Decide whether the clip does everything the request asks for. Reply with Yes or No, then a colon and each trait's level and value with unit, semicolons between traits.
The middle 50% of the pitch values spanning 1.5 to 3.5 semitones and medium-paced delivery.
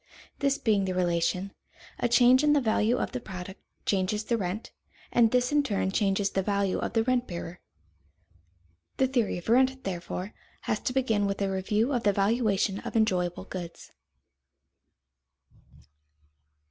No: average, 4.4 semitones; average, 155 wpm